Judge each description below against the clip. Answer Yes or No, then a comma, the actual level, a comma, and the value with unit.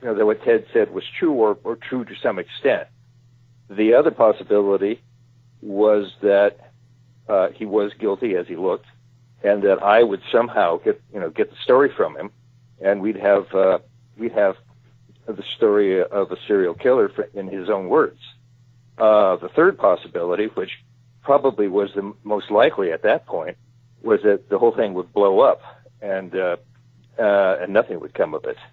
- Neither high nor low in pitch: No, low, 120 Hz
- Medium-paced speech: Yes, average, 180 wpm